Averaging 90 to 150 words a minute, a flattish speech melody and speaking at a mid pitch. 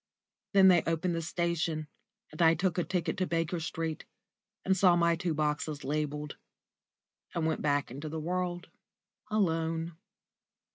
Yes: average, 145 wpm; narrow, 2.1 semitones; medium, 165 Hz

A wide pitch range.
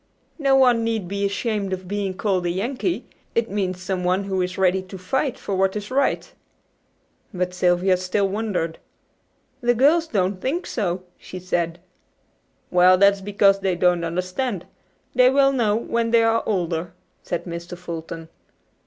No: average, 3.9 semitones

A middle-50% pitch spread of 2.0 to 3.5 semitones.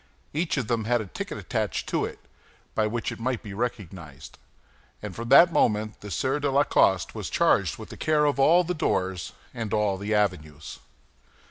No: wide, 5.6 semitones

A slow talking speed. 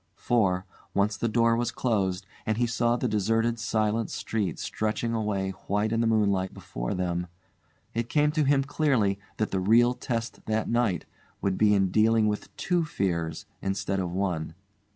No: average, 170 wpm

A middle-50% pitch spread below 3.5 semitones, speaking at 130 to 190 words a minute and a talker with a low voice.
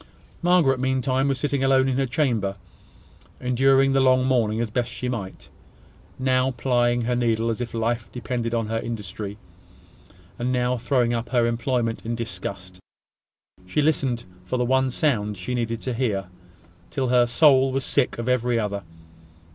Yes: narrow, 2.4 semitones; average, 165 wpm; low, 125 Hz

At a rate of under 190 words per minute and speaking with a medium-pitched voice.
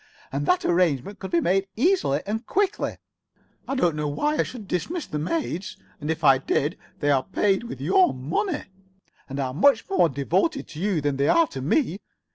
No: average, 200 wpm; medium, 180 Hz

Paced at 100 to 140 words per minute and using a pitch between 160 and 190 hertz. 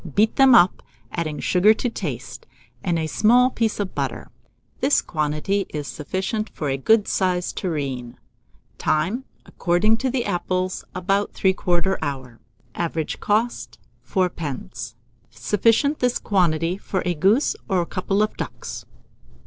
Yes: slow, 135 wpm; medium, 185 Hz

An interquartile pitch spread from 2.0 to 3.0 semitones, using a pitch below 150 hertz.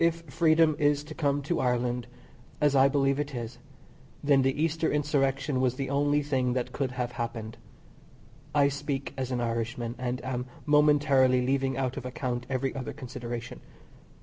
Yes: average, 2.7 semitones; low, 135 Hz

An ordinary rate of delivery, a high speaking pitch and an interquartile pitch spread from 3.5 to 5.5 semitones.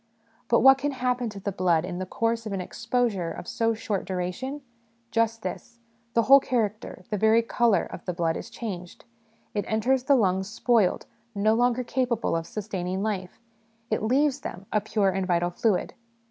Yes: average, 180 wpm; high, 215 Hz; average, 4.3 semitones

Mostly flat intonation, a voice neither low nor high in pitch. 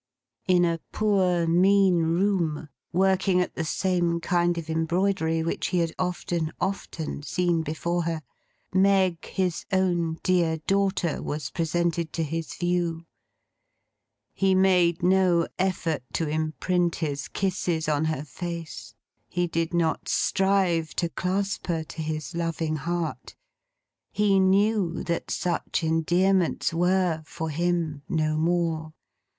Yes: narrow, 2.3 semitones; medium, 170 Hz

